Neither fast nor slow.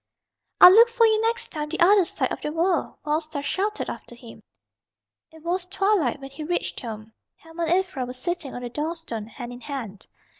No: fast, 210 wpm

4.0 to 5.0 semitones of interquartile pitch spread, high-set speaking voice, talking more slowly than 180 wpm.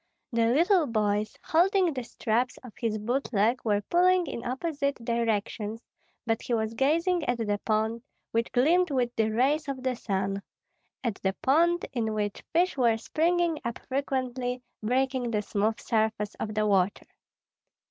Yes: average, 4.4 semitones; high, 240 Hz; average, 155 wpm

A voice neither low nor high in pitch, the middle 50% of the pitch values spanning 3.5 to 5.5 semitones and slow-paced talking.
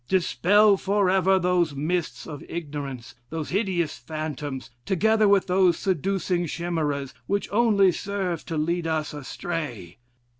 Yes: medium, 175 Hz; average, 4.1 semitones; slow, 120 wpm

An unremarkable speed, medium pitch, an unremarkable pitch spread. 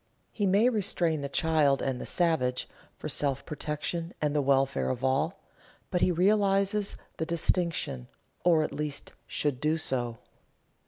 Yes: average, 150 wpm; medium, 155 Hz; average, 4.5 semitones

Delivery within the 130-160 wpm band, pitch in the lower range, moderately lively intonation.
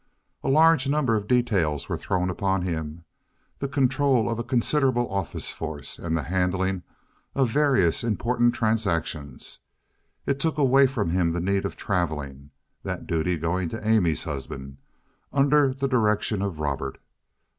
No: average, 145 wpm; low, 100 Hz; wide, 7.5 semitones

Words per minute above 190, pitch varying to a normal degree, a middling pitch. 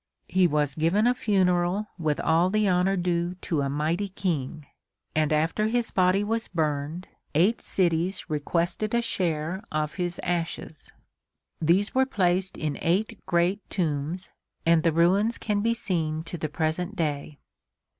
No: average, 150 wpm; average, 3.7 semitones; medium, 175 Hz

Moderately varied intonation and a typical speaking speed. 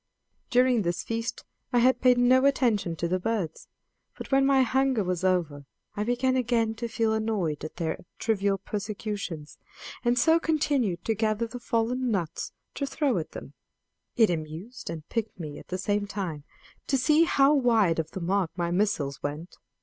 No: wide, 5.8 semitones; average, 175 wpm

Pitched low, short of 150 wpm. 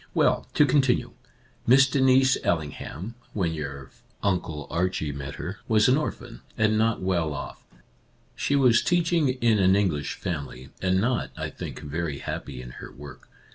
No: very low, 95 Hz; average, 165 wpm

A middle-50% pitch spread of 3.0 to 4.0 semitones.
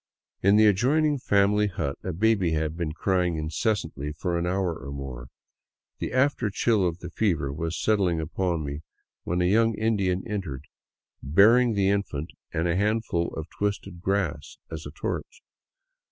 No: average, 4.7 semitones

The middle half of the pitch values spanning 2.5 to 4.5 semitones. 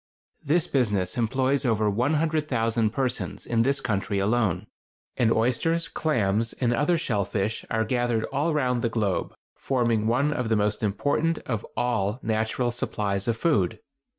Yes: average, 4.1 semitones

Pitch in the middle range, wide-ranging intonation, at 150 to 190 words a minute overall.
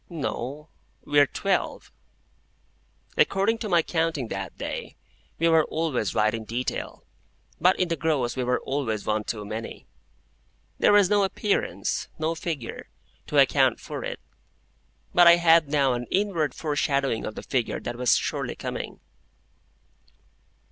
No: medium, 150 Hz; wide, 5.7 semitones; average, 140 wpm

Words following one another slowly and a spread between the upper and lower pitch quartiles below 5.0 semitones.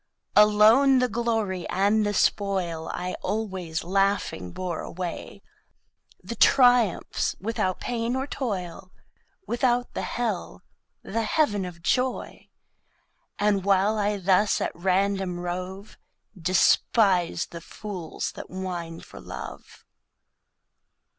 Yes: slow, 110 wpm; average, 3.4 semitones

